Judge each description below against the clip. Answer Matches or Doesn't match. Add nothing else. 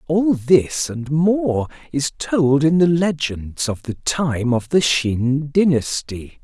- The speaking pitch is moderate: Matches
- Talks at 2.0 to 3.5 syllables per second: Matches